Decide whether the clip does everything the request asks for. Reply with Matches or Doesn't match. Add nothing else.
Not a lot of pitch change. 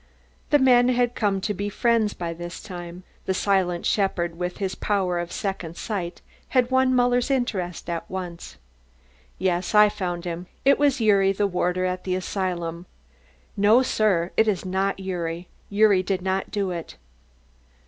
Doesn't match